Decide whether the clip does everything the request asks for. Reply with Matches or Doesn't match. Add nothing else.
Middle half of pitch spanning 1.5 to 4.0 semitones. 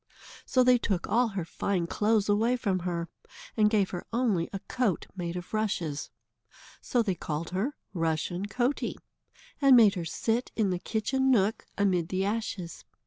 Doesn't match